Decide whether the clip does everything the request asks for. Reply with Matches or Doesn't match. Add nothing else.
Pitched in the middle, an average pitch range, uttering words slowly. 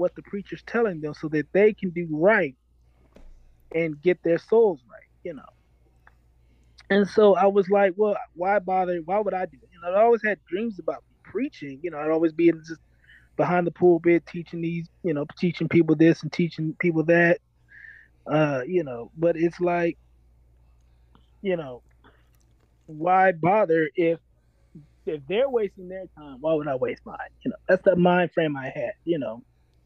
Doesn't match